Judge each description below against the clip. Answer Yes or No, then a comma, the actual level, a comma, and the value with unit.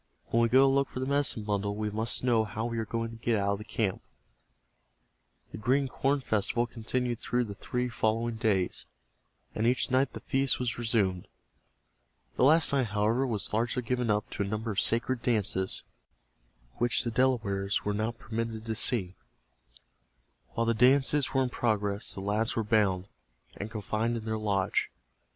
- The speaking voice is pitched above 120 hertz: No, low, 115 Hz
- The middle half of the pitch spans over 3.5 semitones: No, average, 2.8 semitones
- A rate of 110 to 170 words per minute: No, average, 180 wpm